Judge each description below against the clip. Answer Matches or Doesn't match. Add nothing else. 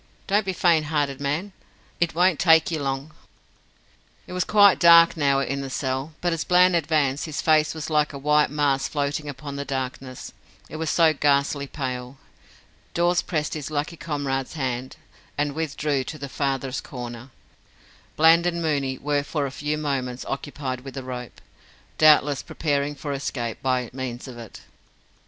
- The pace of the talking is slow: Doesn't match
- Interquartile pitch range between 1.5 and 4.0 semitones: Matches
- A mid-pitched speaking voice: Matches